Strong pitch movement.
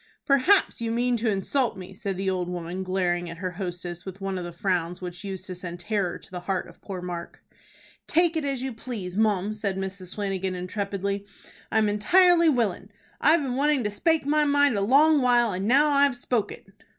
Yes: wide, 5.8 semitones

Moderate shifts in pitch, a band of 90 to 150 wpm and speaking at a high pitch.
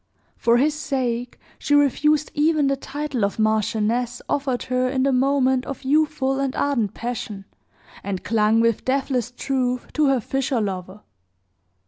Yes: average, 3.2 semitones; average, 145 wpm; very high, 255 Hz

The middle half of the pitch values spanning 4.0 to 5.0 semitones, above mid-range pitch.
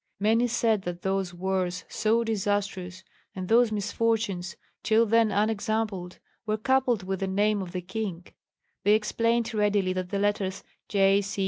No: average, 2.8 semitones; high, 205 Hz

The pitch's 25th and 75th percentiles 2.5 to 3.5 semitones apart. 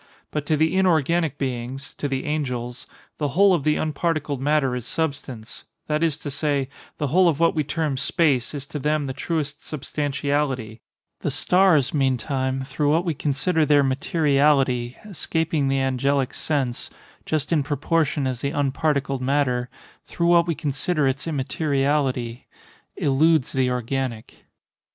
Yes: average, 2.8 semitones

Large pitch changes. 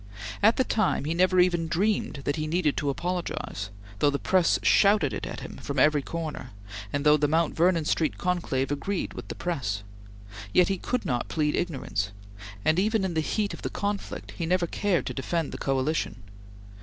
No: average, 4.2 semitones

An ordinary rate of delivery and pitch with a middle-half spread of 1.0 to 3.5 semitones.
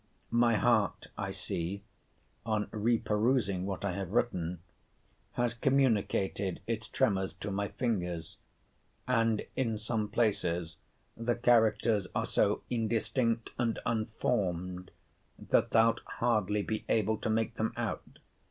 No: slow, 125 wpm; average, 3.0 semitones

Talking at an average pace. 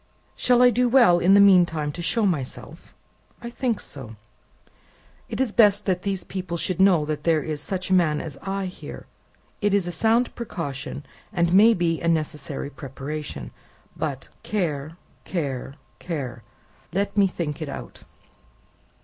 Yes: average, 160 wpm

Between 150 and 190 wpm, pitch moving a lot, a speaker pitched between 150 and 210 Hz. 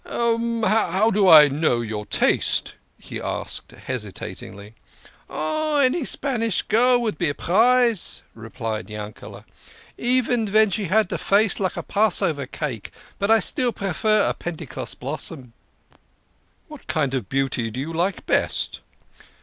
No: average, 140 wpm; wide, 9.0 semitones; medium, 185 Hz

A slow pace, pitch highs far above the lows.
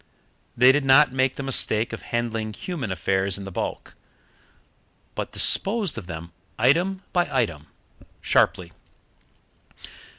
Yes: slow, 125 wpm; wide, 6.7 semitones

